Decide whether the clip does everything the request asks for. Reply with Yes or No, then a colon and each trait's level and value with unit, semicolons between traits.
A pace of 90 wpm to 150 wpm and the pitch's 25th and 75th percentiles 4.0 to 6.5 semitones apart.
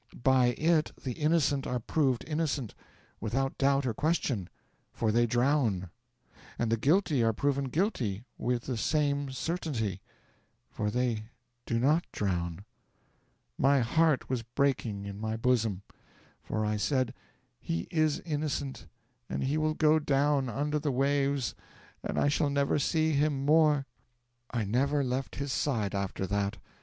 Yes: average, 145 wpm; average, 4.6 semitones